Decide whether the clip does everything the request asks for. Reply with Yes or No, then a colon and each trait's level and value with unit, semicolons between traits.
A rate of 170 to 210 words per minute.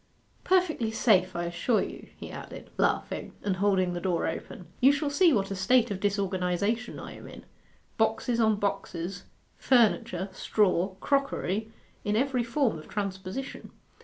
No: average, 150 wpm